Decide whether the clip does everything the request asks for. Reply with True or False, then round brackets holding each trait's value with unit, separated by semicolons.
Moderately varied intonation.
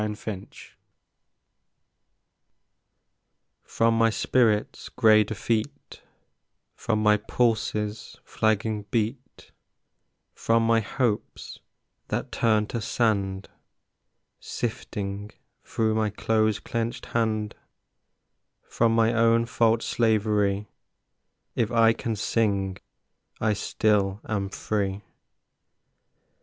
False (1.6 semitones)